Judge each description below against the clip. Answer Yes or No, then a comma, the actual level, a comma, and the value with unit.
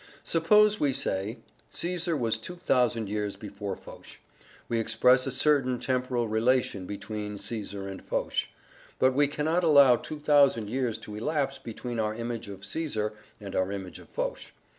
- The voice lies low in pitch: Yes, low, 120 Hz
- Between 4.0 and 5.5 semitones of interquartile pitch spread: Yes, average, 5.1 semitones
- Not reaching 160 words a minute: Yes, average, 150 wpm